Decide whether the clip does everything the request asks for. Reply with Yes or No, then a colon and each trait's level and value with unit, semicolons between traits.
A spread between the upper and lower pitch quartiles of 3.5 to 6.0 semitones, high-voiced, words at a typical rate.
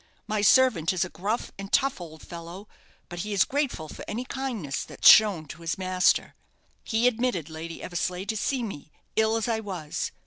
Yes: average, 4.9 semitones; high, 195 Hz; average, 185 wpm